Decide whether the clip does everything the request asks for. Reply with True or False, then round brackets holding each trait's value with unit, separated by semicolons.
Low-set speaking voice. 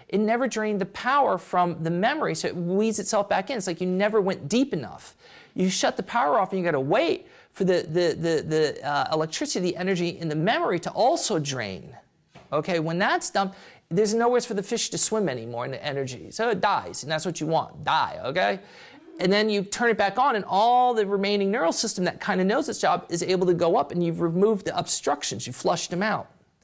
False (195 Hz)